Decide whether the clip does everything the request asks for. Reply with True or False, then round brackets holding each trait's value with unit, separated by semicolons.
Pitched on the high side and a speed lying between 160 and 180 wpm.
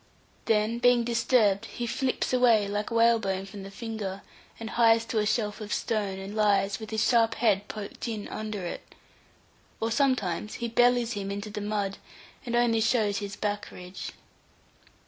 True (215 Hz; 165 wpm)